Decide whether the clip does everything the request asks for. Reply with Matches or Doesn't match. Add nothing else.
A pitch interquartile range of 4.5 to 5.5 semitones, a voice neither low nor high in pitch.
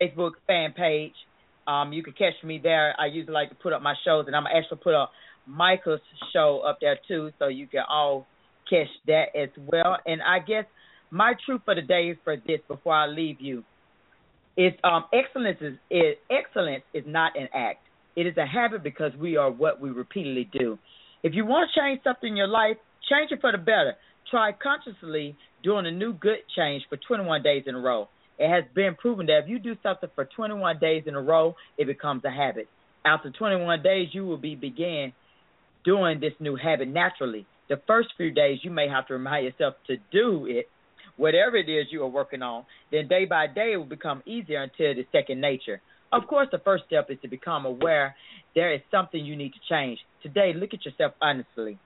Matches